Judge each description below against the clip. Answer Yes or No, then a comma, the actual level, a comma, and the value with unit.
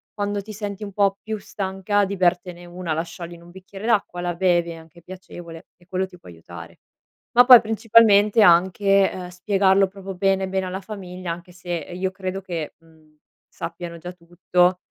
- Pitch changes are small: Yes, narrow, 2.3 semitones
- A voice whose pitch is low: No, medium, 185 Hz